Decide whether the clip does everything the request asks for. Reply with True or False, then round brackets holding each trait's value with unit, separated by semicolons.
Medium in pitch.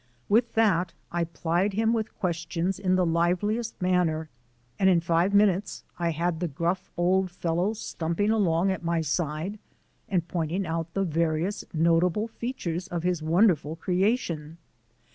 True (175 Hz)